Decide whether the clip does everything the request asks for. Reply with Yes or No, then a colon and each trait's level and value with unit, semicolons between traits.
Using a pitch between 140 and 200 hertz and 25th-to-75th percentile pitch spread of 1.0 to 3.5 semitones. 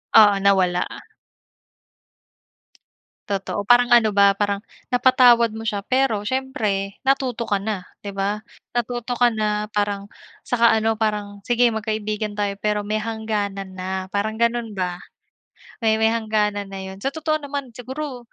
No: high, 215 Hz; average, 3.0 semitones